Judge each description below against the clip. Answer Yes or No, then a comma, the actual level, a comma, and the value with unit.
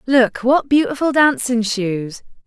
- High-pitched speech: Yes, high, 245 Hz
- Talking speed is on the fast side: No, slow, 120 wpm